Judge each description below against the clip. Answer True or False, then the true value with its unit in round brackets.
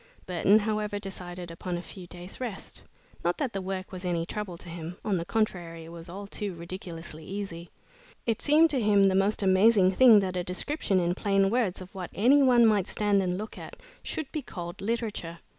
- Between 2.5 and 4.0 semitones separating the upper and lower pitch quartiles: True (3.2 semitones)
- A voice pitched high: True (195 Hz)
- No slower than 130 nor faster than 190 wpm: False (205 wpm)